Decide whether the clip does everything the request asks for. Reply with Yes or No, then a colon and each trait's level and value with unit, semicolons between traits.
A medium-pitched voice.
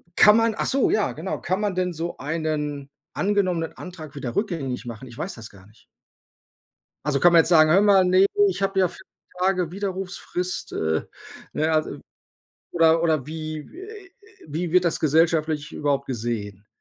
Yes: medium, 165 Hz